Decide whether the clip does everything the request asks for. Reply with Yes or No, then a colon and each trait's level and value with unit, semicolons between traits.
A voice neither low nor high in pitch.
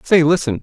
Yes: medium, 155 Hz